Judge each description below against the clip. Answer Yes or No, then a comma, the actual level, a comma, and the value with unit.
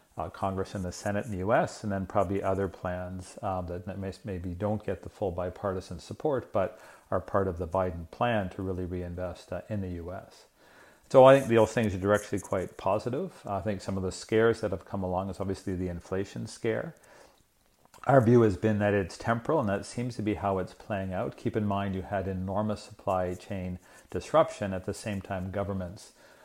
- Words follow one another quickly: Yes, fast, 210 wpm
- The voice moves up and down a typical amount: No, narrow, 2.2 semitones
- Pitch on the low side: Yes, very low, 95 Hz